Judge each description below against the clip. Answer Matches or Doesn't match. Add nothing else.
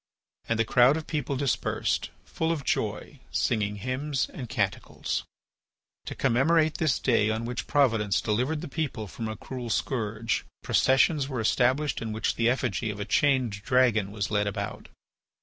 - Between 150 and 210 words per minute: Matches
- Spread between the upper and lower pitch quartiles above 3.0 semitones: Matches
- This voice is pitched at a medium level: Doesn't match